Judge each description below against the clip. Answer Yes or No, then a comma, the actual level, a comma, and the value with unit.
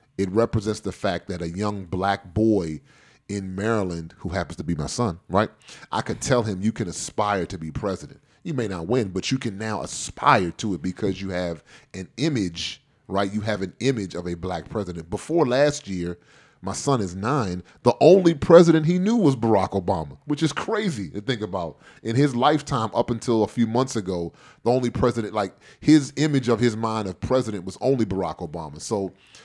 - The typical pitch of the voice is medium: No, low, 105 Hz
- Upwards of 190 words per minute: Yes, average, 200 wpm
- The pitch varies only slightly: No, average, 5.1 semitones